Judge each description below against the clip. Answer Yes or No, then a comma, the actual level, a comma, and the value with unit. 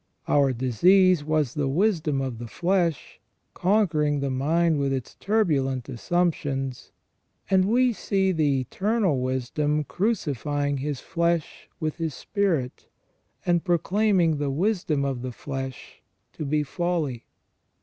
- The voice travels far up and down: No, average, 4.8 semitones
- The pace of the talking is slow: Yes, slow, 125 wpm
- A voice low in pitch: No, medium, 150 Hz